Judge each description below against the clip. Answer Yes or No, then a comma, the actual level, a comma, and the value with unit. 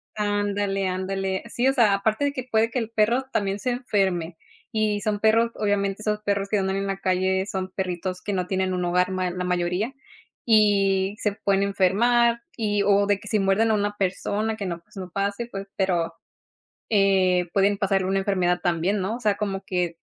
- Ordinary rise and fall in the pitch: No, narrow, 2.0 semitones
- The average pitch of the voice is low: No, high, 195 Hz